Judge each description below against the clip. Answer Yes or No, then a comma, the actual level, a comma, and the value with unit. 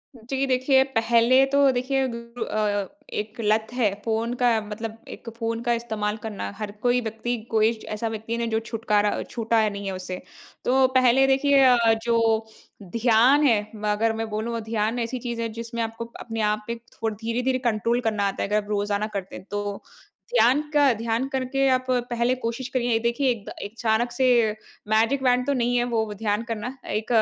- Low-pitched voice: No, high, 230 Hz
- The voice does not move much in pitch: Yes, narrow, 2.3 semitones